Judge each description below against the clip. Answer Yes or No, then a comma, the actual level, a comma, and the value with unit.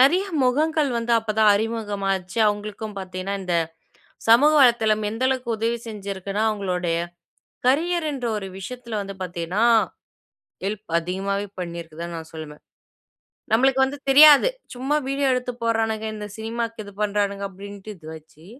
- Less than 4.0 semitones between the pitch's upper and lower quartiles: No, average, 4.3 semitones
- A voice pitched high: Yes, high, 215 Hz